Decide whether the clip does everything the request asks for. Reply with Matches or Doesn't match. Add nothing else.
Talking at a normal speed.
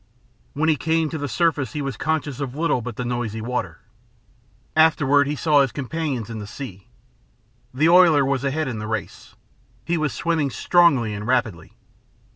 Matches